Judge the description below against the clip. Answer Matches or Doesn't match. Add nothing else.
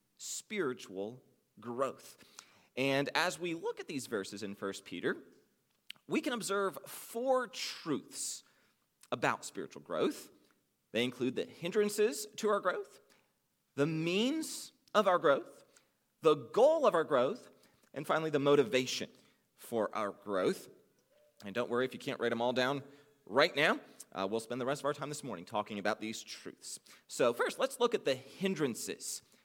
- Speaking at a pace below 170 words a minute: Matches